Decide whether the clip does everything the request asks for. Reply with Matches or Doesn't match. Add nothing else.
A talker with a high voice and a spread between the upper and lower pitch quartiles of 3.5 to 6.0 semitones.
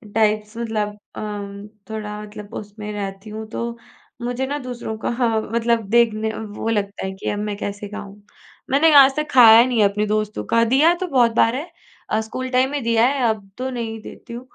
Doesn't match